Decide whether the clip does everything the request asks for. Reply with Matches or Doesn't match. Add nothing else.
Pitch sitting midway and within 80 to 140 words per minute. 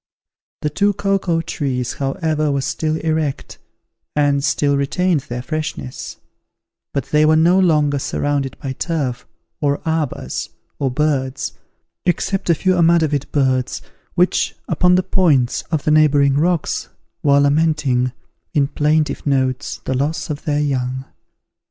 Matches